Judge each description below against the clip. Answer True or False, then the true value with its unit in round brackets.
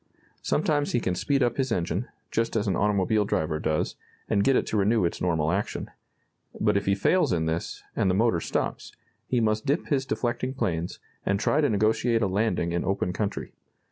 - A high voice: False (105 Hz)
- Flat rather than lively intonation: False (5.0 semitones)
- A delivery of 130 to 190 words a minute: False (200 wpm)